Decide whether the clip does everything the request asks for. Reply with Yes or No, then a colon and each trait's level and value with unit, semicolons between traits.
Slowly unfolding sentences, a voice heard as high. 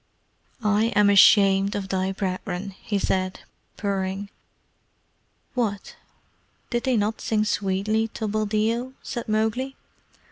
Yes: slow, 110 wpm; high, 205 Hz